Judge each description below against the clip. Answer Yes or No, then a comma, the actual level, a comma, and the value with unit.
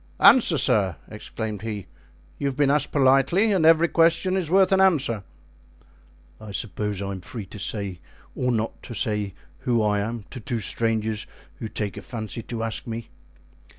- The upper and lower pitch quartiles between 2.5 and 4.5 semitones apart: No, wide, 5.4 semitones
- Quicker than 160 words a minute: Yes, average, 175 wpm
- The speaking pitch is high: No, low, 115 Hz